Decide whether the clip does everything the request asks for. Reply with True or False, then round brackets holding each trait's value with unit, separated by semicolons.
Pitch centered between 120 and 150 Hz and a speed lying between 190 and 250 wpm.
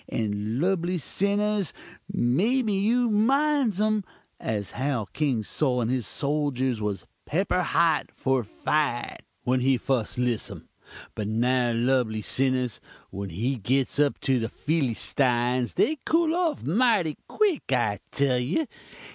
False (135 Hz; 135 wpm)